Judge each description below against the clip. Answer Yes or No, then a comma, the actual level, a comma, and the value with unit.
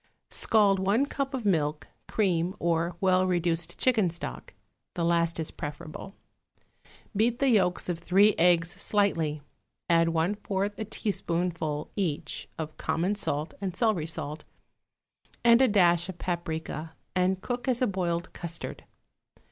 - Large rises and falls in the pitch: No, average, 3.5 semitones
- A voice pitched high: No, medium, 180 Hz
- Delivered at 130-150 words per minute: Yes, average, 140 wpm